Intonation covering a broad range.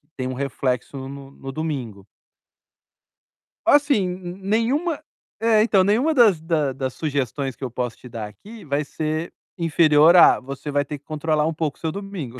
Yes: wide, 5.8 semitones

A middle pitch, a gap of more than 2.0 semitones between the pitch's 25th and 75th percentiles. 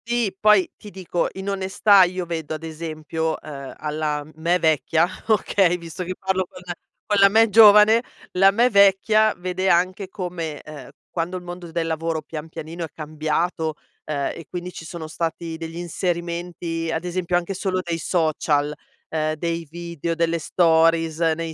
Yes: medium, 170 Hz; narrow, 2.4 semitones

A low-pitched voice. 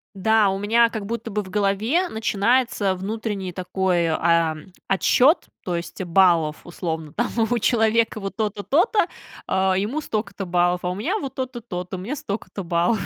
No: high, 200 Hz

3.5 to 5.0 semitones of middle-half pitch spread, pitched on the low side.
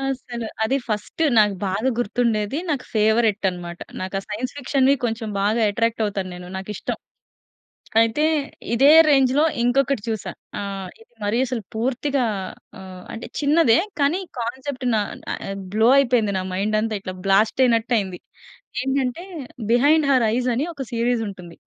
No: average, 4.1 semitones; high, 230 Hz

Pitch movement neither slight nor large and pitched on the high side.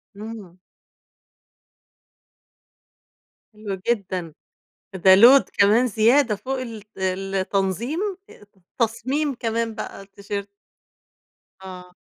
Yes: average, 3.4 semitones; high, 210 Hz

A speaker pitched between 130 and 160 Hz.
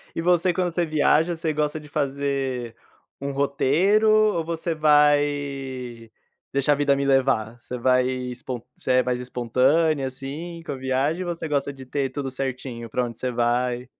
Yes: medium, 140 Hz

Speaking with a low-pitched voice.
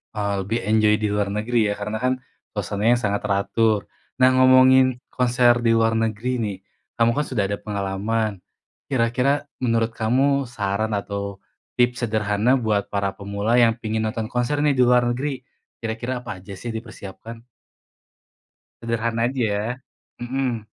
Yes: low, 115 Hz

